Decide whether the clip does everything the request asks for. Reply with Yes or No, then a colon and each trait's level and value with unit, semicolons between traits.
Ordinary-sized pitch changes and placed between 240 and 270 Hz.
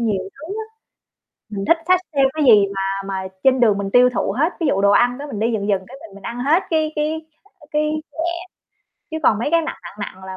No: wide, 7.4 semitones; high, 245 Hz